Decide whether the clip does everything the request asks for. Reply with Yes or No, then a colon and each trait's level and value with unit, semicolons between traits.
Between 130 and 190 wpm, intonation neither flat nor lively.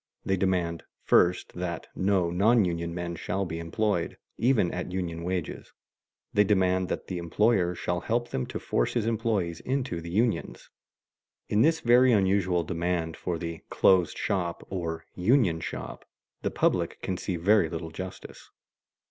Yes: average, 155 wpm; average, 3.5 semitones